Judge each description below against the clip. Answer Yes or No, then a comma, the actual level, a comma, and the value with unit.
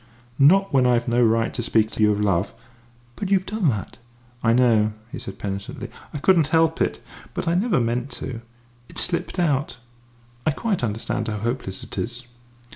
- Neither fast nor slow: Yes, average, 185 wpm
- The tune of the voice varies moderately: No, wide, 6.6 semitones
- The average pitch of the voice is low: Yes, low, 125 Hz